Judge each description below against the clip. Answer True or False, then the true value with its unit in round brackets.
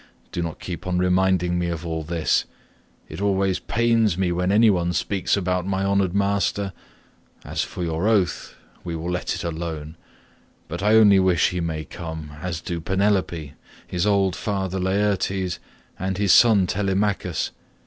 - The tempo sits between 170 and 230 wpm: False (160 wpm)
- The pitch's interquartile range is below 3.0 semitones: True (2.5 semitones)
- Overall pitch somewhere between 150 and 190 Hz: False (90 Hz)